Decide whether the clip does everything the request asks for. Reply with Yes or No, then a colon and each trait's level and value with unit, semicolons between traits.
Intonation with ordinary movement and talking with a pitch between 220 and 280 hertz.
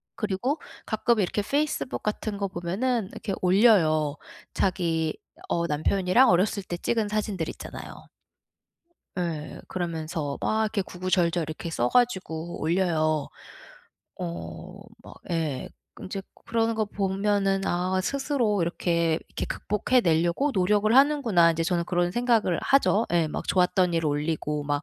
No: average, 4.3 semitones; medium, 185 Hz